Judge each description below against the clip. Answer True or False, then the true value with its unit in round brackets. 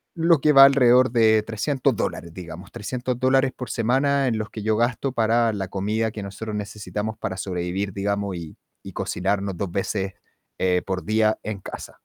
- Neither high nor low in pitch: False (110 Hz)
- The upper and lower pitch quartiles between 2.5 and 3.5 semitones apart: False (4.1 semitones)